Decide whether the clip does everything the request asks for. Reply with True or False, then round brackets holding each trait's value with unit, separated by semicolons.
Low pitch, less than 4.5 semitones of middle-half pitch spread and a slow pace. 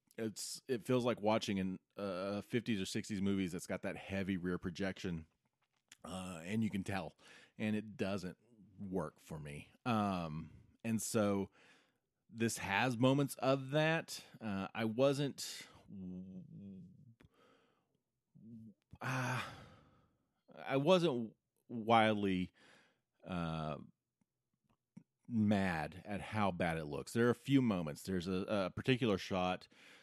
True (100 Hz; 4.1 semitones; 120 wpm)